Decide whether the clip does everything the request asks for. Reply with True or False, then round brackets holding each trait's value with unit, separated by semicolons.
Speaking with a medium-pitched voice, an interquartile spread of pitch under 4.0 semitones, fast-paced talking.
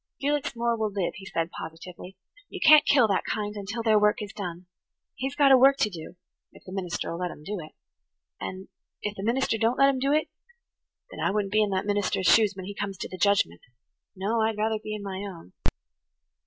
False (205 Hz; 3.3 semitones; 210 wpm)